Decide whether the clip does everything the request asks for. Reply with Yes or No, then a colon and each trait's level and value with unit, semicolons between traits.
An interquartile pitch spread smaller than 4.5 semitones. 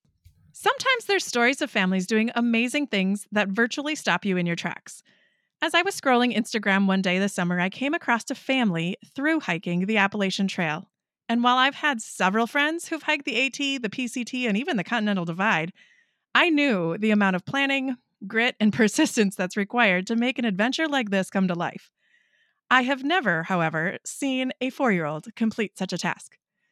No: wide, 5.6 semitones